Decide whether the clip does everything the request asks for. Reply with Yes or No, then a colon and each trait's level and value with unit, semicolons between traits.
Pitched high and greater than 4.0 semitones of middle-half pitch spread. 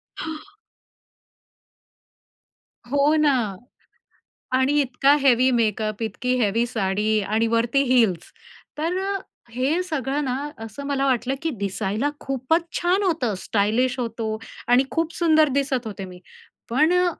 Yes: very high, 255 Hz; average, 5.0 semitones